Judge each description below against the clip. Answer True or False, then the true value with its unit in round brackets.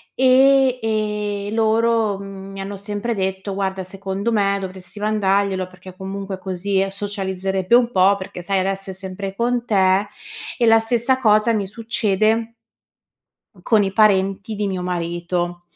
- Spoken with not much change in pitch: True (2.3 semitones)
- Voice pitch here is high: True (200 Hz)